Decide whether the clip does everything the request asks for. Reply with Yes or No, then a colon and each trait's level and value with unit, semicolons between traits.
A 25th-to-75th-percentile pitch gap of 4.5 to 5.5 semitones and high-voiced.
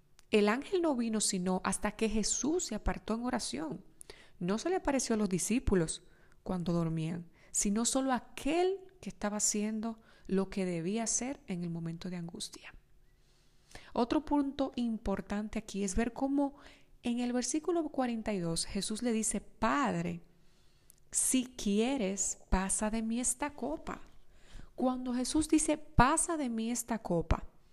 Yes: average, 5.2 semitones; high, 225 Hz